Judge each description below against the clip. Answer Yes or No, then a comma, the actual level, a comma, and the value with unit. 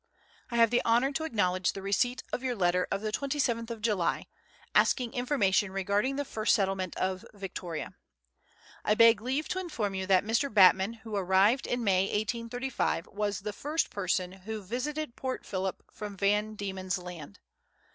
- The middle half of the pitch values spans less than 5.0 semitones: Yes, average, 4.3 semitones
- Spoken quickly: No, average, 170 wpm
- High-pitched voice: Yes, high, 210 Hz